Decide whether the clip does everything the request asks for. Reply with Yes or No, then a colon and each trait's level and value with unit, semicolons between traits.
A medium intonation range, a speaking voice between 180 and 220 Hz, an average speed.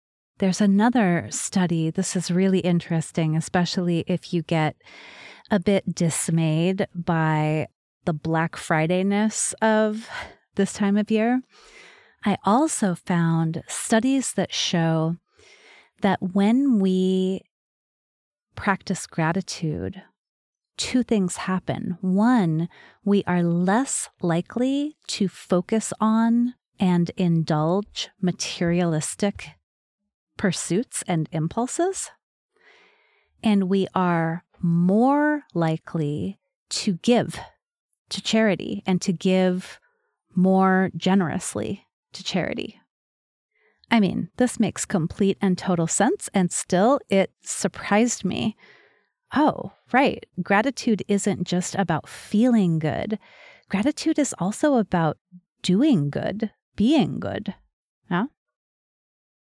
No: average, 4.3 semitones; high, 190 Hz; slow, 100 wpm